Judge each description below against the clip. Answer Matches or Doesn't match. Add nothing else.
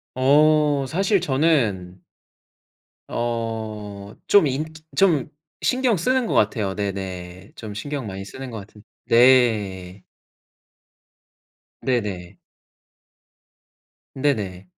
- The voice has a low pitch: Matches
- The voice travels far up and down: Matches